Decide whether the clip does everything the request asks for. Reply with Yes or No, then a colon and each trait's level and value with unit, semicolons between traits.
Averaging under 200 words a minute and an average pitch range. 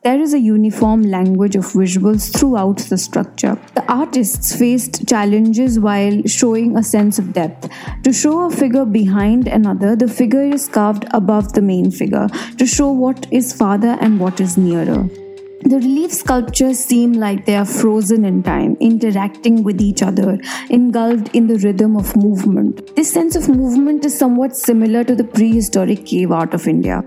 Yes: average, 170 wpm; average, 3.8 semitones